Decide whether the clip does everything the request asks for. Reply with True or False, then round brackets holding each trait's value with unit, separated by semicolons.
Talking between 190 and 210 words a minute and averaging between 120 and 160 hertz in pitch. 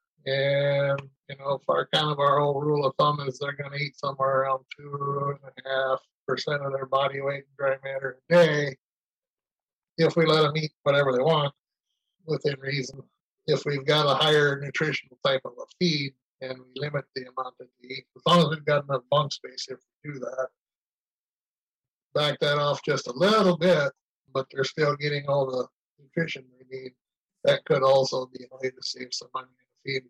True (205 wpm; 140 Hz)